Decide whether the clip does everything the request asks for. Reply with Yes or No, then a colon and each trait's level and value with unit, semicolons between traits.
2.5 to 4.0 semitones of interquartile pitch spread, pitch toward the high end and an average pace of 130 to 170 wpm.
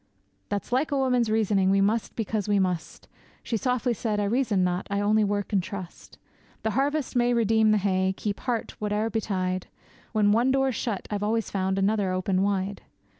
No: average, 2.9 semitones; high, 210 Hz; average, 185 wpm